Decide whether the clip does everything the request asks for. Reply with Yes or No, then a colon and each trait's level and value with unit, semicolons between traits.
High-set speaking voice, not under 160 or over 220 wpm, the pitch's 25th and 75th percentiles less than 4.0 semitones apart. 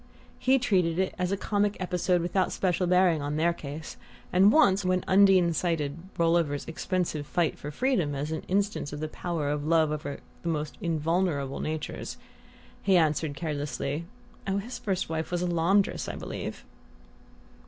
No: medium, 170 Hz; average, 165 wpm; average, 3.5 semitones